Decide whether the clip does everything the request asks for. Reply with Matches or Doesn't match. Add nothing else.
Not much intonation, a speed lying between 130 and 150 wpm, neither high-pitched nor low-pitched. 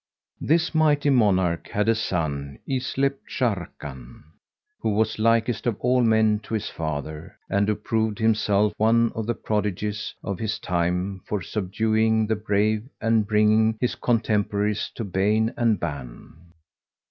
Doesn't match